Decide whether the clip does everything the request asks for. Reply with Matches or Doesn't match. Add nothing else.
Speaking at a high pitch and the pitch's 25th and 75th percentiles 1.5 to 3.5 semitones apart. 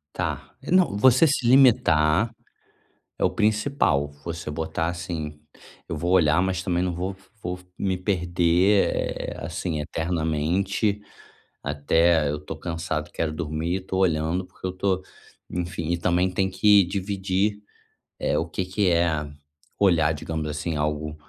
Doesn't match